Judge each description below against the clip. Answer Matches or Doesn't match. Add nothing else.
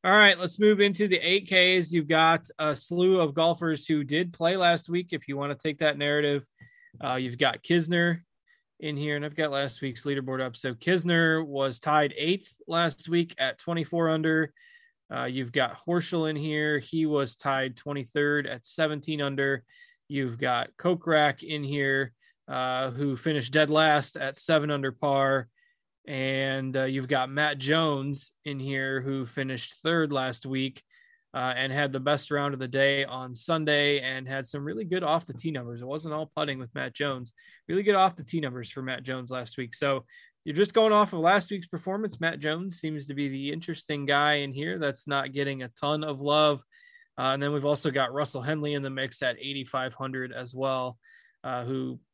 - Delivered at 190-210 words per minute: Matches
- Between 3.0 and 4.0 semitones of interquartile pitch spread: Matches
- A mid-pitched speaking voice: Matches